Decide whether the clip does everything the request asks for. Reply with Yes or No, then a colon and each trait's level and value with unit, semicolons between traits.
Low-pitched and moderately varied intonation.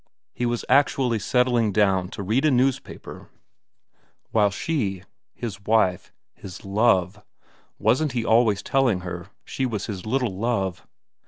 Yes: low, 110 Hz; average, 4.3 semitones